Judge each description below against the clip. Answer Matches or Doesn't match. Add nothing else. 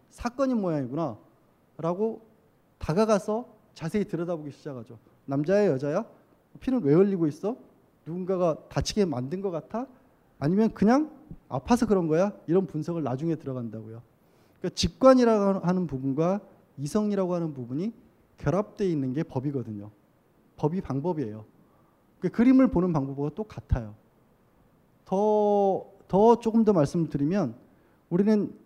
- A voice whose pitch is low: Doesn't match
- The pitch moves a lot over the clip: Matches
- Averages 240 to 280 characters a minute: Doesn't match